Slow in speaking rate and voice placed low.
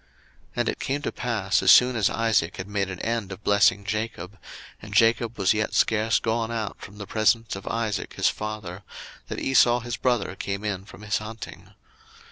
No: average, 195 wpm; low, 110 Hz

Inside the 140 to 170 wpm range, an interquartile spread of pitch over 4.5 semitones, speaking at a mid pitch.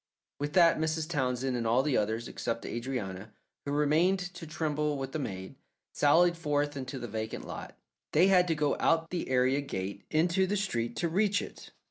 No: average, 185 wpm; average, 5.0 semitones; medium, 145 Hz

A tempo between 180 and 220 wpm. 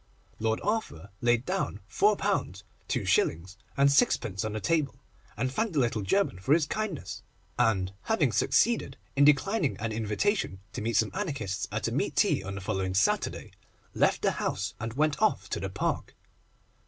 No: average, 160 wpm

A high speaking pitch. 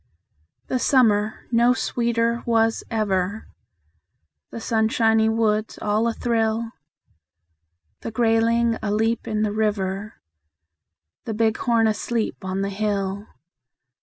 Yes: high, 220 Hz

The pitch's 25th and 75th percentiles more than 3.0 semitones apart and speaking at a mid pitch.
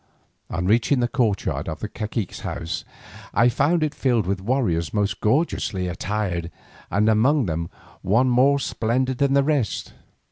No: average, 5.2 semitones; low, 110 Hz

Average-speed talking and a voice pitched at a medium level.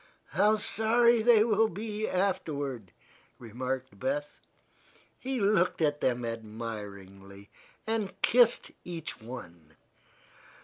No: slow, 95 wpm; medium, 165 Hz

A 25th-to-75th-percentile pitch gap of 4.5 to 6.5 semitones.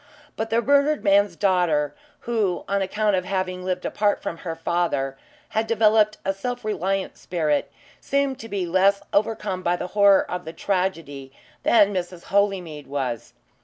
No: average, 3.3 semitones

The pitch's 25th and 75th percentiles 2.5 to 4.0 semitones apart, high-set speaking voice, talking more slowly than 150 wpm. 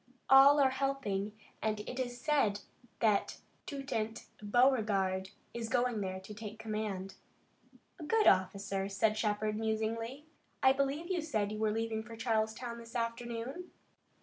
Yes: average, 3.7 semitones; high, 225 Hz; average, 140 wpm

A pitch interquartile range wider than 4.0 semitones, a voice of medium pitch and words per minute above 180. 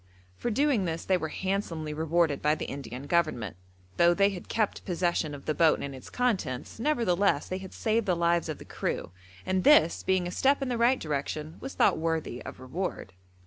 Yes: average, 4.5 semitones; medium, 170 Hz; average, 200 wpm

